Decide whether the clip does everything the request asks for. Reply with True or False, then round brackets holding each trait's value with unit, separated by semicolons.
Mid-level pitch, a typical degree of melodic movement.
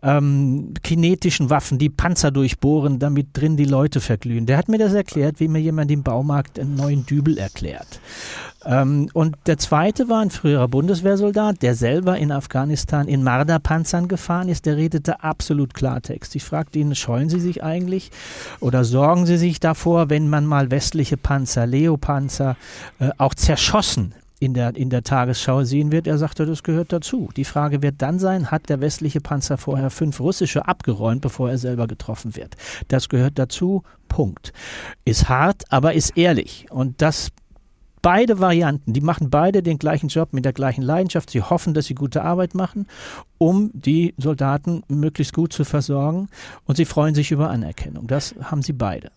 True (150 Hz; 3.5 semitones)